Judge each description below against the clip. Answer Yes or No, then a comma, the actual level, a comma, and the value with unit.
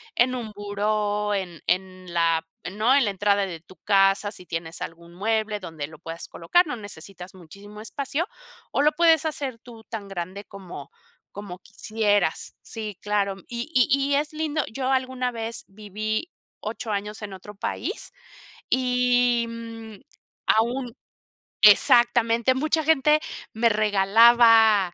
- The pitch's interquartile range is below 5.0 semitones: Yes, average, 4.0 semitones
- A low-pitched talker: No, high, 215 Hz